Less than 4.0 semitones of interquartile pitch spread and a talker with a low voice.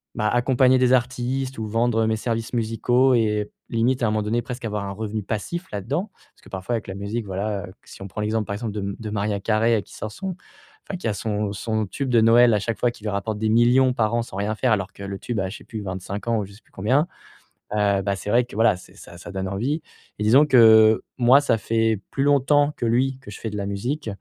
Yes: average, 2.9 semitones; low, 110 Hz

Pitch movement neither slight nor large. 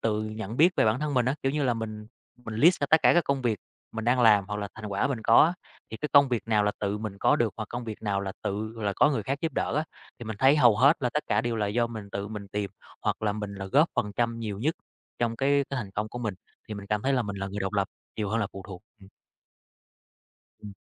Yes: average, 3.6 semitones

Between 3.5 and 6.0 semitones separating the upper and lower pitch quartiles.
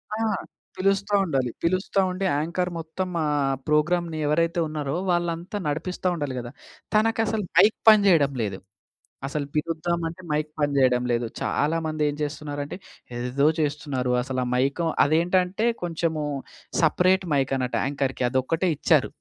Yes: average, 4.0 semitones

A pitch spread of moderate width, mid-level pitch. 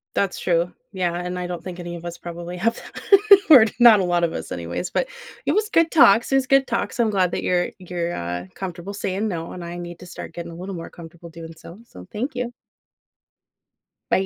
Yes: average, 3.1 semitones; medium, 180 Hz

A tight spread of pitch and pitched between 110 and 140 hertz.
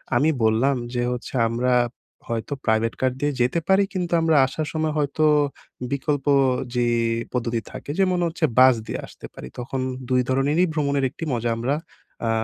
No: average, 4.2 semitones; low, 135 Hz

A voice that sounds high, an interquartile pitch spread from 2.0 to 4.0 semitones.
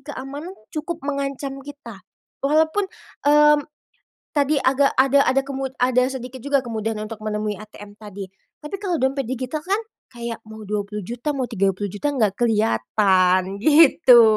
No: very high, 255 Hz; average, 5.1 semitones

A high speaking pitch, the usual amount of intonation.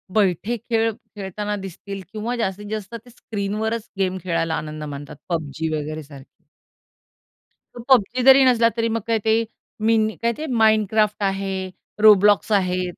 Yes: high, 210 Hz; average, 3.6 semitones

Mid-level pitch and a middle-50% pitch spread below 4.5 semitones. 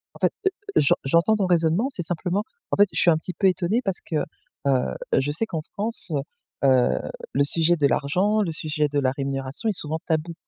No: medium, 165 Hz; average, 5.0 semitones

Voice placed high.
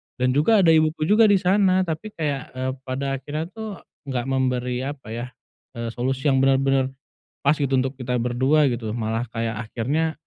No: low, 135 Hz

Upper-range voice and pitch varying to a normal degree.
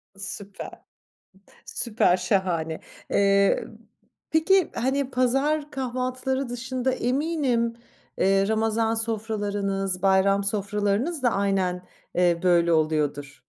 Yes: high, 205 Hz; average, 4.9 semitones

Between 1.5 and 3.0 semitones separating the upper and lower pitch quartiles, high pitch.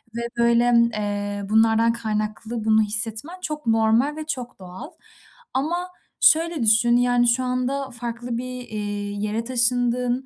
Yes: average, 2.7 semitones; high, 235 Hz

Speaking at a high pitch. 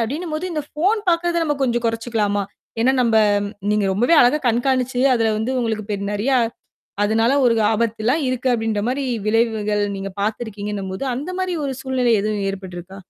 Yes: high, 230 Hz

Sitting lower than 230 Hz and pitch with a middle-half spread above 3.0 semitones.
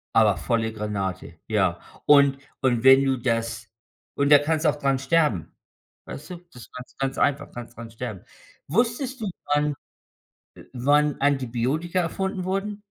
Yes: low, 135 Hz; average, 4.8 semitones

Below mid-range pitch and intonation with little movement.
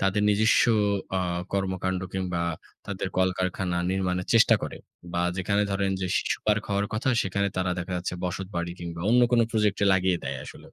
Yes: very low, 95 Hz; narrow, 1.9 semitones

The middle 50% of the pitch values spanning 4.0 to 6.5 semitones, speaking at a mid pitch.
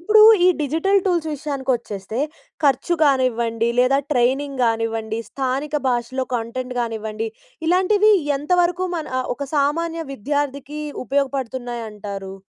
No: average, 4.4 semitones; very high, 265 Hz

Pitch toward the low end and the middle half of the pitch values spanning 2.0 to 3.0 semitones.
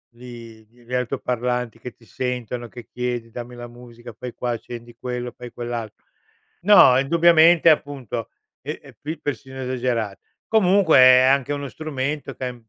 Yes: low, 125 Hz; narrow, 2.5 semitones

